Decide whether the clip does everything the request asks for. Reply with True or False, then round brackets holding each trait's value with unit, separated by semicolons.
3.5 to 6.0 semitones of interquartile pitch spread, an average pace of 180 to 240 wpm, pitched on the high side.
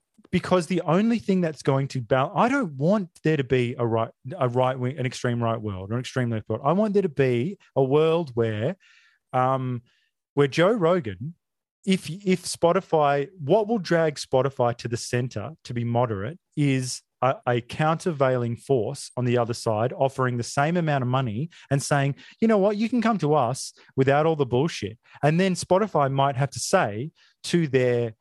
False (5.5 semitones; 195 wpm; 140 Hz)